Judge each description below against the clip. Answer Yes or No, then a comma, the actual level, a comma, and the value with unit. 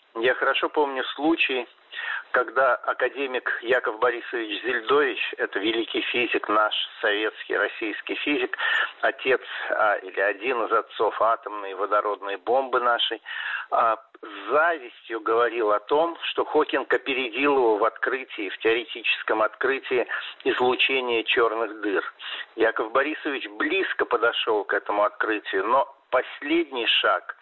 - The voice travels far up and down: Yes, wide, 5.9 semitones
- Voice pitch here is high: Yes, very high, 370 Hz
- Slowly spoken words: No, average, 120 wpm